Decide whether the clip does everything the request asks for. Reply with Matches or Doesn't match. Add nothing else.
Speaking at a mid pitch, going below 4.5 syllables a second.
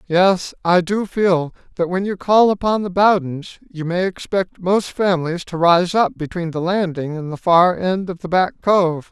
Matches